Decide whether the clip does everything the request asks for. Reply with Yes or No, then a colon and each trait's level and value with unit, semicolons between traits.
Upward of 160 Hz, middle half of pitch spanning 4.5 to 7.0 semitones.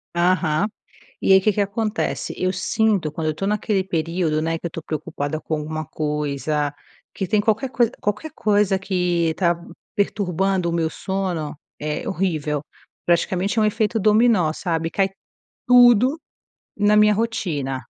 Yes: medium, 185 Hz; average, 4.8 semitones